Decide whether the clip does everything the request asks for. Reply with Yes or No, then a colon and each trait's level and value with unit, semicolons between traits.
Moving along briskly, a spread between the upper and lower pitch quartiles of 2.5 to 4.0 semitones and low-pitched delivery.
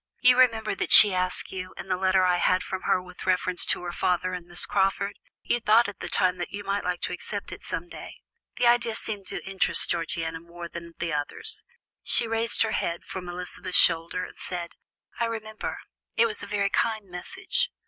No: fast, 210 wpm; average, 3.5 semitones; medium, 185 Hz